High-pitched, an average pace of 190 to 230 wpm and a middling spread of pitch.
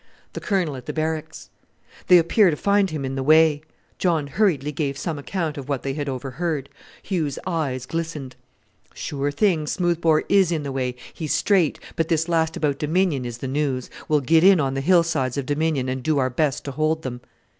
No: medium, 155 Hz; average, 200 wpm; average, 3.4 semitones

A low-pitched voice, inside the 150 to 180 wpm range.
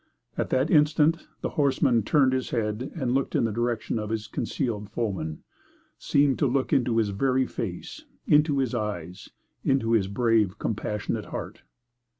Yes: low, 120 Hz; average, 155 wpm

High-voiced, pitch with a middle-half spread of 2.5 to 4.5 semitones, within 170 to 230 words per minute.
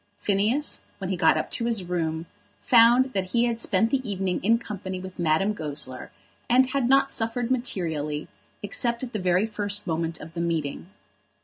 No: high, 195 Hz; wide, 5.6 semitones; average, 180 wpm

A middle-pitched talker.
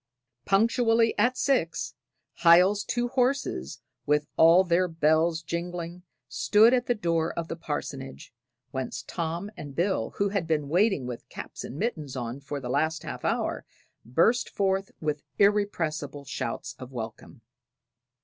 Yes: medium, 170 Hz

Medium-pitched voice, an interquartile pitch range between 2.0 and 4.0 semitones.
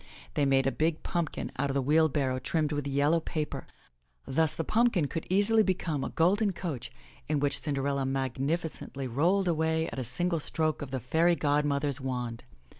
Yes: medium, 150 Hz; average, 3.4 semitones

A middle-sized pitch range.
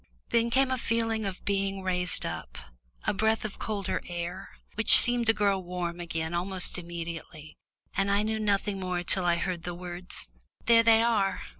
Yes: average, 3.8 semitones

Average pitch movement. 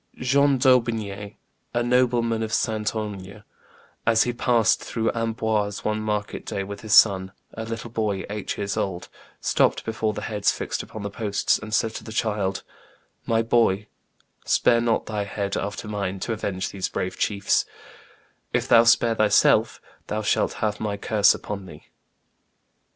No: narrow, 2.0 semitones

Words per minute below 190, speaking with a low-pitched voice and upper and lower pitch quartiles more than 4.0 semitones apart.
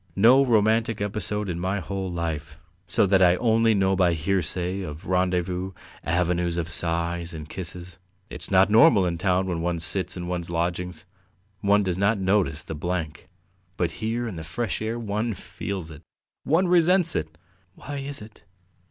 No: average, 170 wpm; very low, 95 Hz; average, 3.6 semitones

